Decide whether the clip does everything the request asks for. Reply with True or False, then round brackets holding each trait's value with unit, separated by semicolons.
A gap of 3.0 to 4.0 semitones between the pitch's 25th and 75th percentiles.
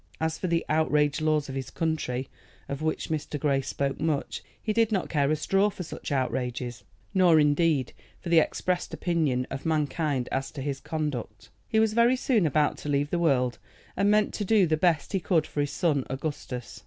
True (3.7 semitones)